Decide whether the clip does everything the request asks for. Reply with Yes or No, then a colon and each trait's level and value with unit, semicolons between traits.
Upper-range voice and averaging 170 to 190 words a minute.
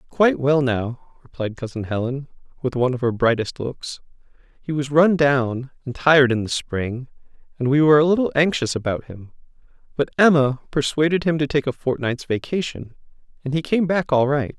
No: medium, 140 Hz; average, 180 wpm